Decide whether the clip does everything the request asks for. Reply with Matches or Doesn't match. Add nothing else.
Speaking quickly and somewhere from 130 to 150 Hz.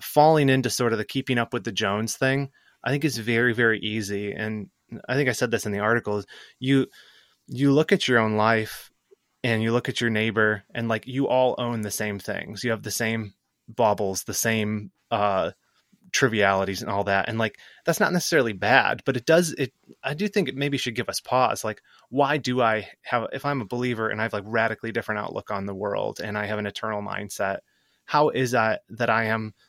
Doesn't match